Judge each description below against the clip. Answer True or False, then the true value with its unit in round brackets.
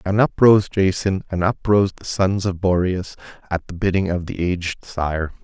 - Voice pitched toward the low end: True (95 Hz)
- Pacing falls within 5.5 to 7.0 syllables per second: False (4.7 syllables/s)